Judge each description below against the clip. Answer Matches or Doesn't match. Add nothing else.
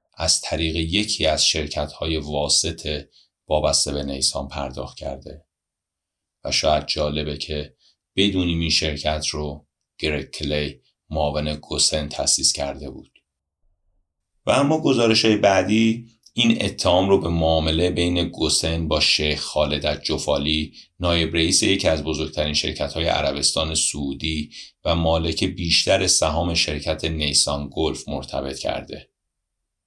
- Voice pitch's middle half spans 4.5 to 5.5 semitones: Doesn't match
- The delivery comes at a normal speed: Matches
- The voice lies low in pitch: Matches